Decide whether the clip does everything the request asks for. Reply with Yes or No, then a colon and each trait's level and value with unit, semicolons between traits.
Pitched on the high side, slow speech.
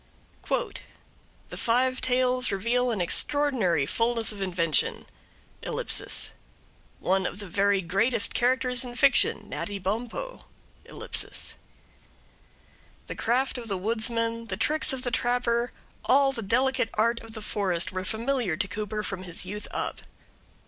Yes: high, 230 Hz; slow, 130 wpm